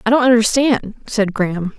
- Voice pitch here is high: Yes, high, 225 Hz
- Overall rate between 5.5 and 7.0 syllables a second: No, 5.1 syllables/s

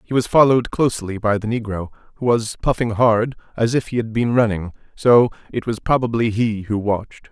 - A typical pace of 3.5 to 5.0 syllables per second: No, 5.5 syllables/s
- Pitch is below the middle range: Yes, low, 115 Hz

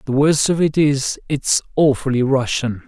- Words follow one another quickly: No, average, 165 wpm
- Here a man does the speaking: Yes, male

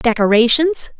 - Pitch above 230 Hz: Yes, very high, 255 Hz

